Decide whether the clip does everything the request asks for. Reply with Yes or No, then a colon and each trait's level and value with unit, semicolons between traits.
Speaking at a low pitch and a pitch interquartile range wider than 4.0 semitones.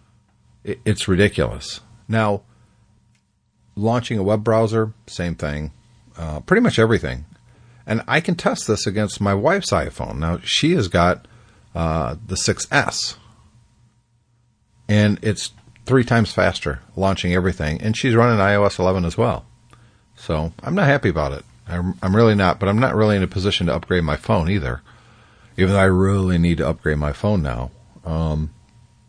Yes: low, 105 Hz; average, 4.8 semitones